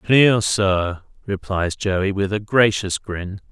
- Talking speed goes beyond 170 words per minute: No, slow, 135 wpm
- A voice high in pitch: No, low, 100 Hz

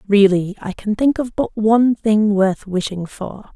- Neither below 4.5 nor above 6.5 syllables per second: No, 4.3 syllables/s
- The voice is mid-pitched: No, high, 210 Hz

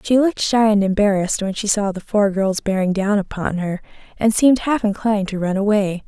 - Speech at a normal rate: No, fast, 215 wpm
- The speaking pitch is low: No, high, 205 Hz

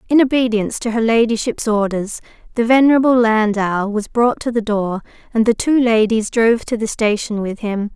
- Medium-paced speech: Yes, average, 180 wpm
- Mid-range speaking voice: No, high, 225 Hz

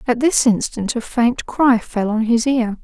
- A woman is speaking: Yes, female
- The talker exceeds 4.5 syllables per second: No, 4.1 syllables/s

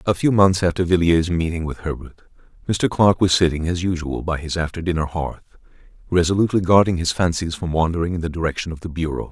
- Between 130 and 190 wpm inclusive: No, average, 200 wpm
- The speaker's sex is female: No, male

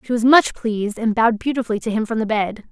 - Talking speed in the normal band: No, fast, 265 wpm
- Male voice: No, female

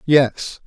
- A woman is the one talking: No, male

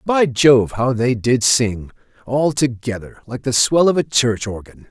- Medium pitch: No, low, 125 Hz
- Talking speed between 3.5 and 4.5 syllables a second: Yes, 4.1 syllables/s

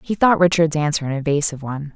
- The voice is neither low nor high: Yes, medium, 155 Hz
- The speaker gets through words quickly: Yes, fast, 215 wpm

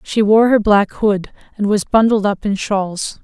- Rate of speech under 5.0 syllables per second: Yes, 4.2 syllables/s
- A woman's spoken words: Yes, female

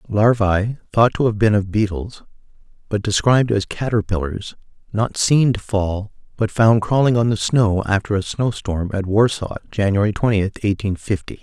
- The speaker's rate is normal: Yes, average, 160 wpm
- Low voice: Yes, low, 105 Hz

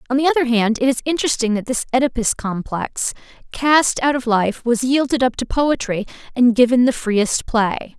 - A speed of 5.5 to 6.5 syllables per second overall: No, 5.0 syllables/s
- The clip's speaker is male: No, female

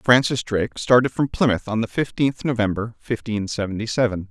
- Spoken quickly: No, average, 180 wpm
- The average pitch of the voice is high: No, low, 115 Hz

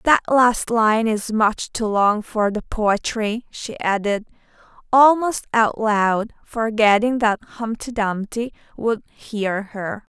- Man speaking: No, female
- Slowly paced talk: Yes, slow, 130 wpm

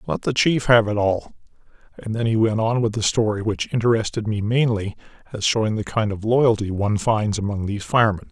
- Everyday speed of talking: No, fast, 210 wpm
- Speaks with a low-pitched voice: Yes, low, 110 Hz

